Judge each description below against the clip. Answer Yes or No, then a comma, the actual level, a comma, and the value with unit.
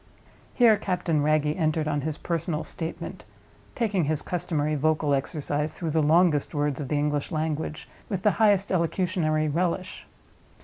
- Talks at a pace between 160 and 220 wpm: No, average, 145 wpm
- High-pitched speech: No, medium, 155 Hz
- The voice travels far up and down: No, average, 3.1 semitones